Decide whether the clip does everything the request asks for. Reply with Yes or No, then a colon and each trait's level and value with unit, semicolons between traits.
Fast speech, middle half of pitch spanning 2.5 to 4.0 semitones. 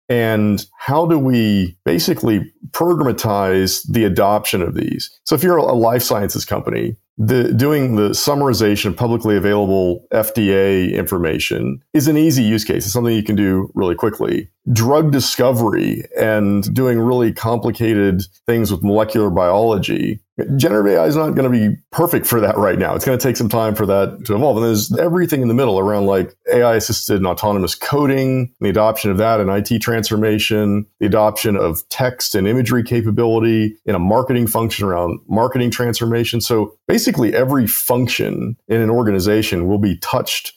No: average, 170 wpm; average, 3.1 semitones